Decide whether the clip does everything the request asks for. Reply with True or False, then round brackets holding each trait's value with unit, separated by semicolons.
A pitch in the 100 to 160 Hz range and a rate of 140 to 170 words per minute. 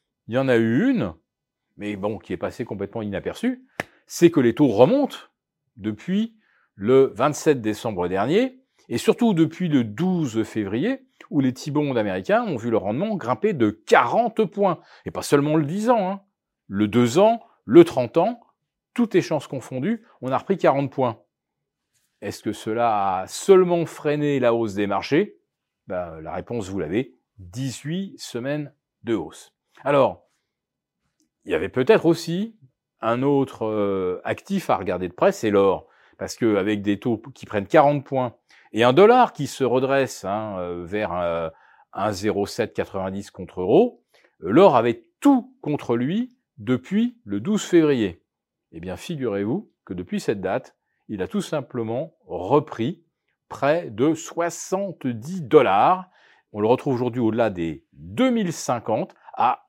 True (140 Hz; 150 wpm)